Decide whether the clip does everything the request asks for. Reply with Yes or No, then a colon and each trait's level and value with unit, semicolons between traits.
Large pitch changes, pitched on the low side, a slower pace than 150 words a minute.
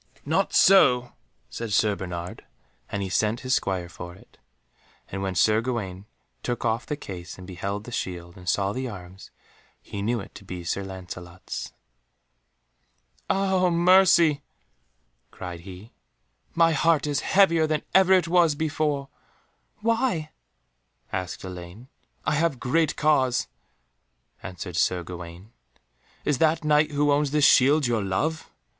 Yes: wide, 8.7 semitones; low, 120 Hz; average, 140 wpm